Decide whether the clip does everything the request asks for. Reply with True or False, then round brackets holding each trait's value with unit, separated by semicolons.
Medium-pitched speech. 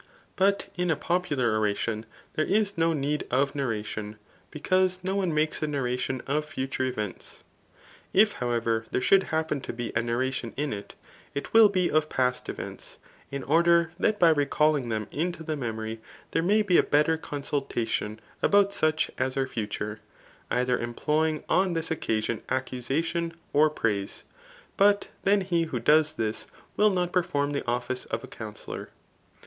True (145 Hz)